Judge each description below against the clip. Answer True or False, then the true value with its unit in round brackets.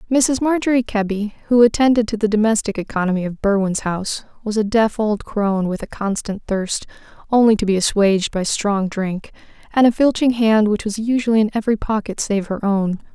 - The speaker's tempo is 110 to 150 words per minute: False (185 wpm)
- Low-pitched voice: False (215 Hz)